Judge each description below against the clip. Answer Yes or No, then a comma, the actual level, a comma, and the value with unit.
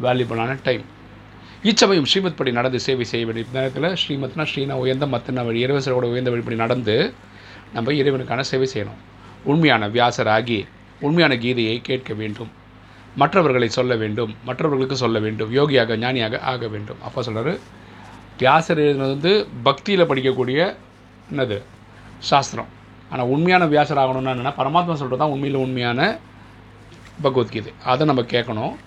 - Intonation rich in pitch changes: No, average, 3.4 semitones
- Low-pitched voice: Yes, low, 125 Hz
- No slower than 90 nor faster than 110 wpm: No, average, 125 wpm